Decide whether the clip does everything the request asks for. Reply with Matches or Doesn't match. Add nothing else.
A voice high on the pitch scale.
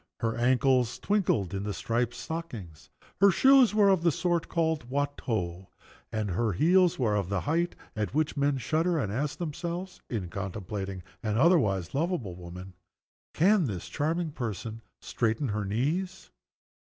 Doesn't match